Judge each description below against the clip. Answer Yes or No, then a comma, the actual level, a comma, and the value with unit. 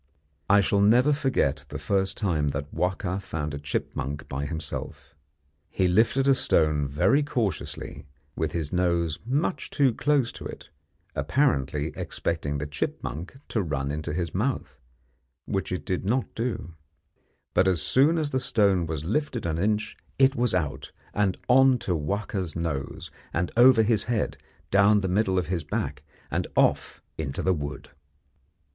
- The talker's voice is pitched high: No, very low, 95 Hz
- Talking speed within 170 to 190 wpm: No, average, 155 wpm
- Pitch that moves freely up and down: Yes, wide, 7.1 semitones